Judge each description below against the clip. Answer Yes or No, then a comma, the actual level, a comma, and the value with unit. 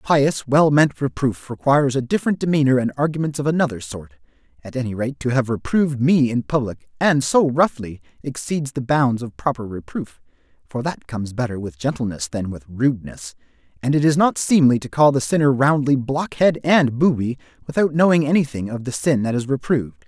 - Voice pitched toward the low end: Yes, low, 130 Hz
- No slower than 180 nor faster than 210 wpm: Yes, average, 185 wpm